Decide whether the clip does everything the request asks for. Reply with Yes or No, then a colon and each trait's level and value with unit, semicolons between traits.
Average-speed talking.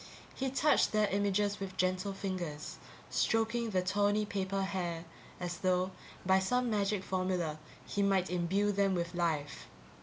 Yes: average, 145 wpm